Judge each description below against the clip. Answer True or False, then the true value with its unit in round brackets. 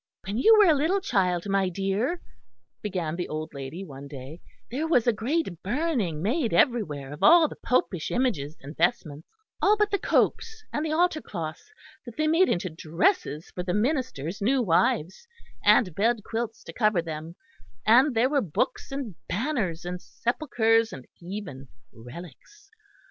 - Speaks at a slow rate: False (165 wpm)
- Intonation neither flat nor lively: False (8.8 semitones)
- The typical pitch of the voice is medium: False (210 Hz)